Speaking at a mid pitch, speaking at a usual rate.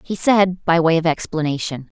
Yes: medium, 165 Hz; average, 180 wpm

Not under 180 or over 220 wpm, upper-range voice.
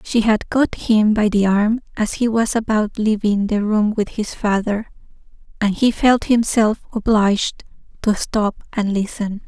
No: average, 165 wpm; high, 215 Hz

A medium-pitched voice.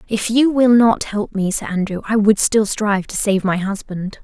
No: high, 210 Hz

